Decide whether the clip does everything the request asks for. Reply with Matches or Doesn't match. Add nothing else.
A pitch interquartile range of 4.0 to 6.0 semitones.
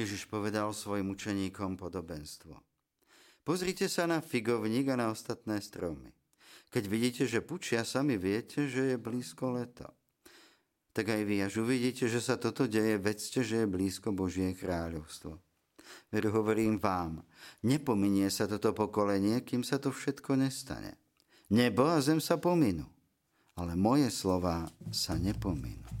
Matches